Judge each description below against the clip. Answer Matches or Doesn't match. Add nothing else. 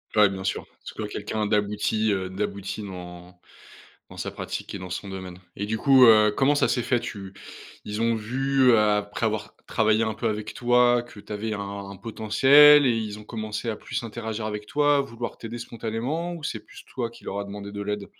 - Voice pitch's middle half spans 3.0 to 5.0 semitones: Doesn't match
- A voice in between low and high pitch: Doesn't match